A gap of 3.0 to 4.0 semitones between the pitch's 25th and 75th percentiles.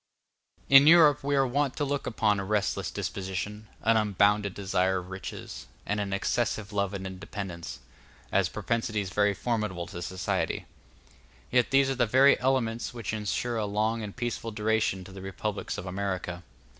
Yes: average, 3.6 semitones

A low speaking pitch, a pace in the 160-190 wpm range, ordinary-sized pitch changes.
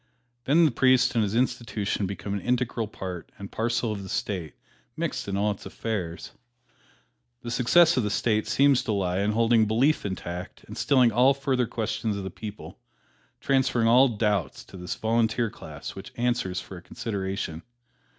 Yes: low, 110 Hz; average, 170 wpm; average, 3.7 semitones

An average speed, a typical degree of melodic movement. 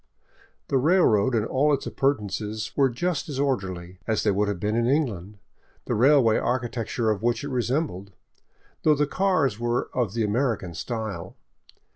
Yes: average, 165 wpm; average, 4.8 semitones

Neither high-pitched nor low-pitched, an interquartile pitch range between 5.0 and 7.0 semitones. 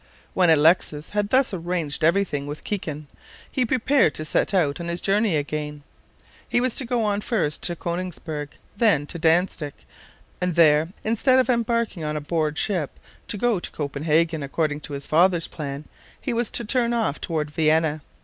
Yes: medium, 170 Hz; wide, 5.6 semitones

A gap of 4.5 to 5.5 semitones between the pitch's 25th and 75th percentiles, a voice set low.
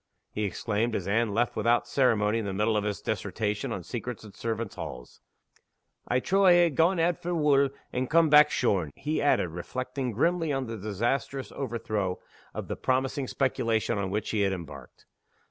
Yes: average, 4.9 semitones; low, 115 Hz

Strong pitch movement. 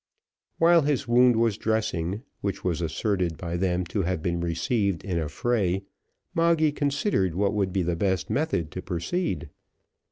Yes: wide, 5.8 semitones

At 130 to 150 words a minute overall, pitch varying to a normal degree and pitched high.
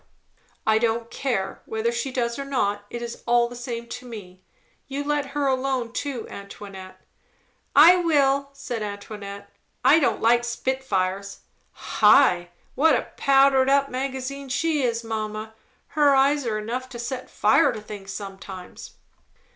Yes: average, 145 wpm; average, 4.3 semitones; high, 240 Hz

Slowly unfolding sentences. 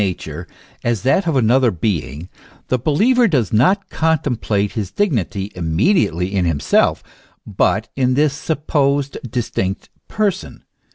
Yes: slow, 130 wpm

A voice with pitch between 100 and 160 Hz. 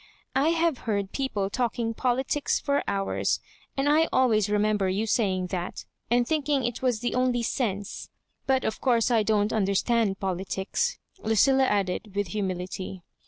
No: high, 220 Hz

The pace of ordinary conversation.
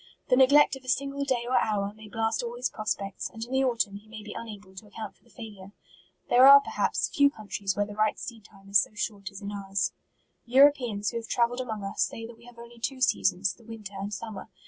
No: fast, 240 wpm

